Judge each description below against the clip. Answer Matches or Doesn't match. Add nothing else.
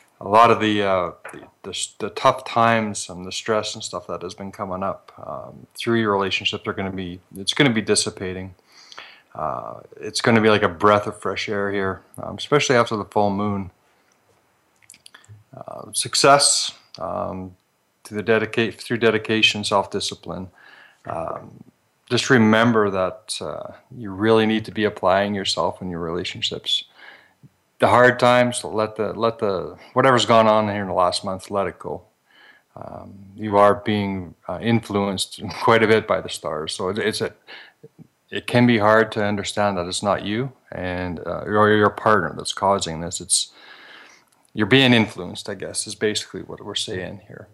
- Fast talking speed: Doesn't match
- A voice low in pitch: Matches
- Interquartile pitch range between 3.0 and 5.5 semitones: Doesn't match